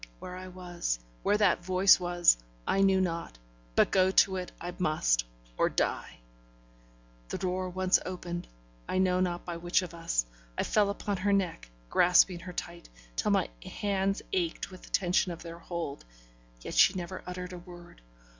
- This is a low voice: No, medium, 180 Hz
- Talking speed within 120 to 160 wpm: No, average, 175 wpm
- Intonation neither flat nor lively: No, narrow, 1.4 semitones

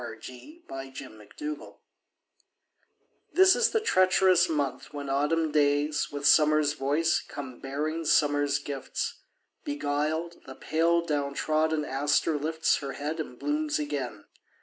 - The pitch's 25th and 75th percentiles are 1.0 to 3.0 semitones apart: Yes, narrow, 2.4 semitones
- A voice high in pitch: No, medium, 150 Hz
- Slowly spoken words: Yes, slow, 125 wpm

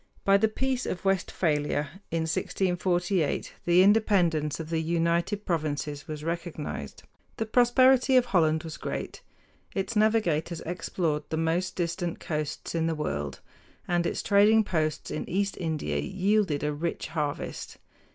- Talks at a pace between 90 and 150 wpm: Yes, average, 140 wpm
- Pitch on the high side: No, medium, 170 Hz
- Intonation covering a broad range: No, average, 4.2 semitones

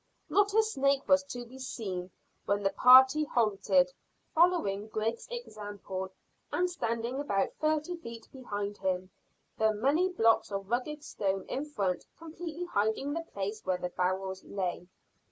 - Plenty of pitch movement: Yes, wide, 7.2 semitones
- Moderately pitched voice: No, high, 230 Hz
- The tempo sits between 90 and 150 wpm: Yes, average, 145 wpm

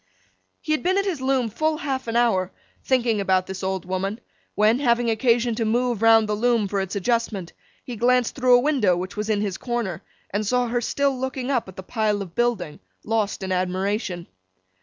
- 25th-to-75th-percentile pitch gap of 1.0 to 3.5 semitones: No, average, 4.2 semitones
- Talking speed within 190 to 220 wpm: Yes, average, 200 wpm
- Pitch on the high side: Yes, high, 225 Hz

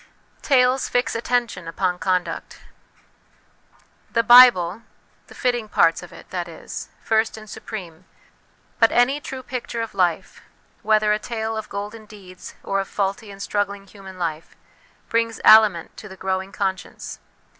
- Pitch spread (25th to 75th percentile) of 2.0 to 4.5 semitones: Yes, average, 3.5 semitones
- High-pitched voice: Yes, high, 210 Hz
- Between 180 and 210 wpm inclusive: No, average, 145 wpm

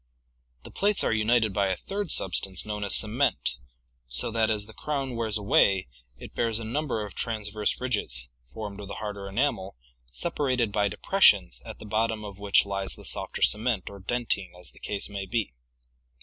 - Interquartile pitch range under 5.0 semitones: Yes, average, 2.8 semitones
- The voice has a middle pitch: No, low, 105 Hz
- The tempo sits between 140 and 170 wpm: No, average, 185 wpm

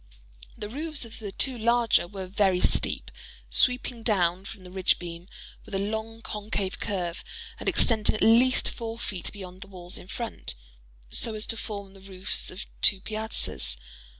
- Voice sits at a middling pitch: No, high, 205 Hz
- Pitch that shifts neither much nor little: Yes, average, 3.2 semitones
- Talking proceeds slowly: No, average, 165 wpm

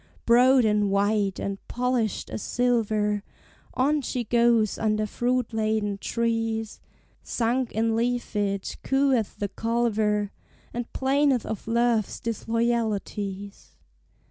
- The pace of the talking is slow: Yes, slow, 105 wpm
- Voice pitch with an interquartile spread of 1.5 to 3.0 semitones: Yes, narrow, 2.5 semitones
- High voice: Yes, high, 225 Hz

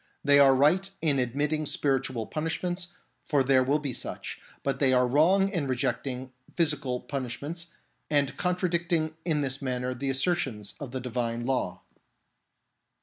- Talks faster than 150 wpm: No, average, 145 wpm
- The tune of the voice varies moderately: Yes, average, 3.7 semitones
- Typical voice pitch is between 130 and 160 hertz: Yes, medium, 140 Hz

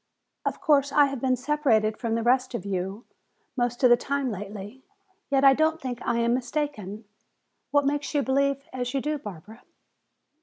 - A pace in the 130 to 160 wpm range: No, average, 180 wpm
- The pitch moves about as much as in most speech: Yes, average, 3.8 semitones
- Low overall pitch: No, very high, 255 Hz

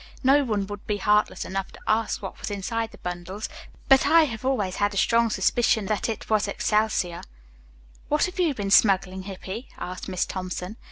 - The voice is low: No, high, 210 Hz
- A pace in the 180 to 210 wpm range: Yes, average, 185 wpm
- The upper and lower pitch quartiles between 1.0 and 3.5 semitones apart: Yes, average, 3.2 semitones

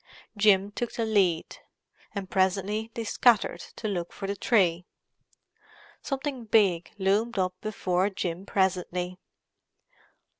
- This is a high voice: Yes, high, 195 Hz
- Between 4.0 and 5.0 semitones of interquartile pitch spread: No, average, 2.9 semitones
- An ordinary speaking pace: No, slow, 115 wpm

